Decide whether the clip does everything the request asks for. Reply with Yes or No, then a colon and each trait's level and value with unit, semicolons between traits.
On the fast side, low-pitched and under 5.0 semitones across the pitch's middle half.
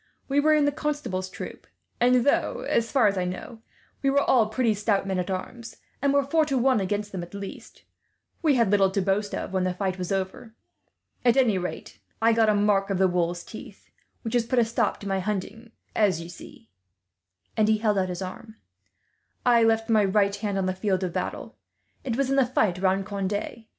No: fast, 215 wpm; high, 210 Hz; average, 3.8 semitones